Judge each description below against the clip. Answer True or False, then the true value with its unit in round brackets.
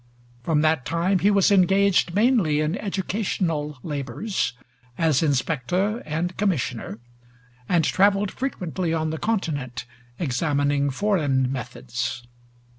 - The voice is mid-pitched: True (160 Hz)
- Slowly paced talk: True (110 wpm)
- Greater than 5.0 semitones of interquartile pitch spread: True (5.5 semitones)